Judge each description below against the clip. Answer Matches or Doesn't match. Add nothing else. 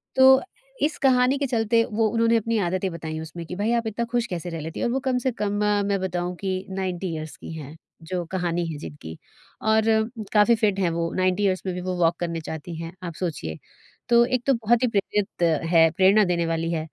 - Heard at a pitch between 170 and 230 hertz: Matches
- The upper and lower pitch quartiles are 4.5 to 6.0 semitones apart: Matches